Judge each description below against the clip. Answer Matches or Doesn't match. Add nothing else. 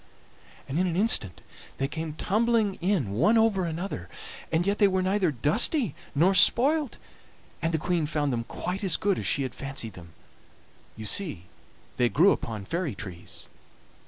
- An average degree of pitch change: Doesn't match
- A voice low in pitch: Doesn't match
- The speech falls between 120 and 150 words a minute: Doesn't match